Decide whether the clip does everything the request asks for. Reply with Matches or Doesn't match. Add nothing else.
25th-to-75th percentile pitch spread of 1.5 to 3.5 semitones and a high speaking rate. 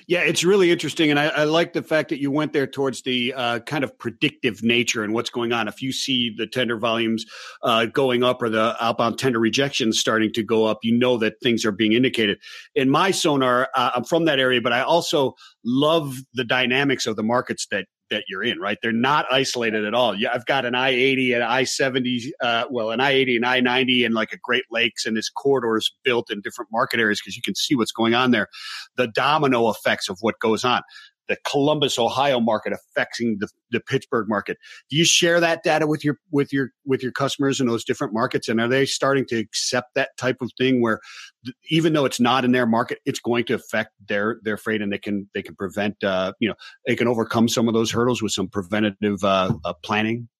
Matches